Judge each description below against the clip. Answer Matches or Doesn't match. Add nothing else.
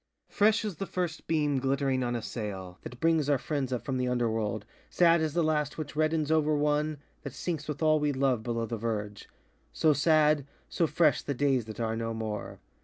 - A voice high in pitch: Doesn't match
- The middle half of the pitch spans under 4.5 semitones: Doesn't match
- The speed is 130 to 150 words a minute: Doesn't match